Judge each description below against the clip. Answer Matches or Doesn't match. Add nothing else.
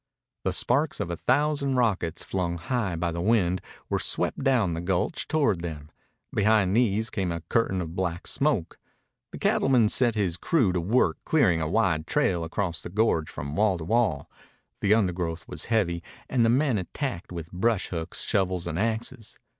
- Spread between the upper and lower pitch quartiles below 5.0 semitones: Doesn't match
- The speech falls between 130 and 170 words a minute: Doesn't match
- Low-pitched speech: Matches